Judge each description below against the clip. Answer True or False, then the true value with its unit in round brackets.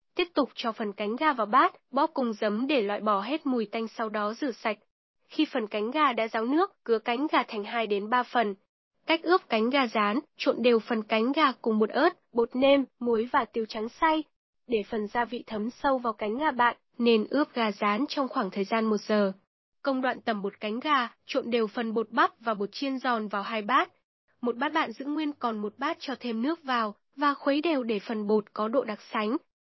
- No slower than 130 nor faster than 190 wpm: False (235 wpm)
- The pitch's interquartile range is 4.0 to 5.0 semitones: True (4.3 semitones)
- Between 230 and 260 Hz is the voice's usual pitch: True (240 Hz)